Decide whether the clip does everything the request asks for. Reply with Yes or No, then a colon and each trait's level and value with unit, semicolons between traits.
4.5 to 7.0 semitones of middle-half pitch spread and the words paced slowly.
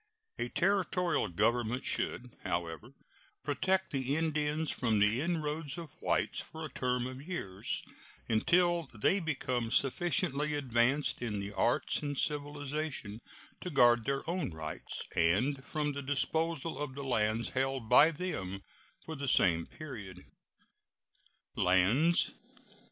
Yes: average, 5.3 semitones; slow, 125 wpm